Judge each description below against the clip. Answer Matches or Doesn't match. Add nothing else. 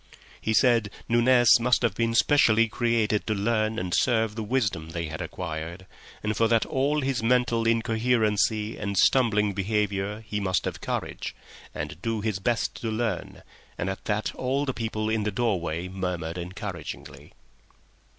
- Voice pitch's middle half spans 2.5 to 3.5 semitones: Matches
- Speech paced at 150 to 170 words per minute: Matches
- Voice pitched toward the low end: Matches